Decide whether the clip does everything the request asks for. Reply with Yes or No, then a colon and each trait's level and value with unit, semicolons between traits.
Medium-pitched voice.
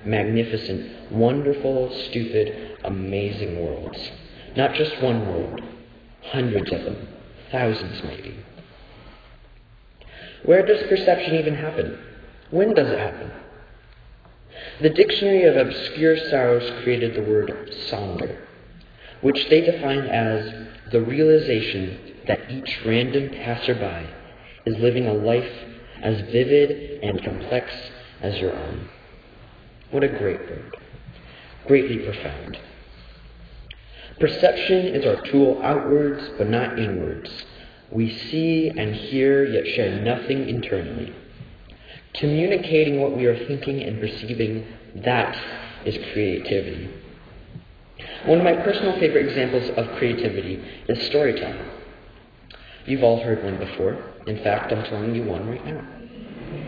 No: low, 120 Hz